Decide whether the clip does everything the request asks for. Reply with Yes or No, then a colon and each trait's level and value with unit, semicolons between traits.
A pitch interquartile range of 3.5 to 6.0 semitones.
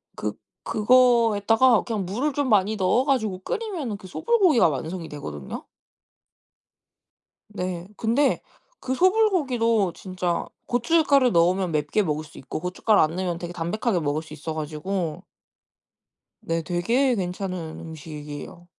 No: wide, 6.6 semitones